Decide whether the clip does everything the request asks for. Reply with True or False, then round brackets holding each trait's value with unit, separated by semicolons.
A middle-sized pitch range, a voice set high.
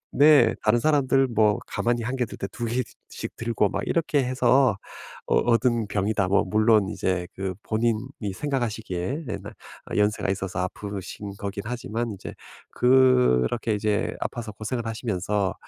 False (3.5 semitones; 110 Hz)